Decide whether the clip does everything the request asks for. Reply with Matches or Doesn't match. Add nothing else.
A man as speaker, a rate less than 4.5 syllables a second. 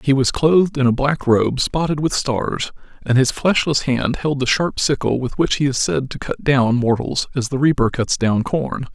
Doesn't match